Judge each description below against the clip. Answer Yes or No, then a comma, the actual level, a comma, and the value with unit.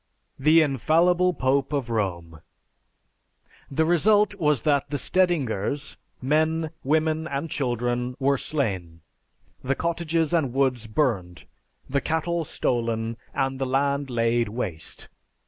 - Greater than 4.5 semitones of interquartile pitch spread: Yes, average, 5.0 semitones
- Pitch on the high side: No, medium, 140 Hz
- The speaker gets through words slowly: Yes, slow, 115 wpm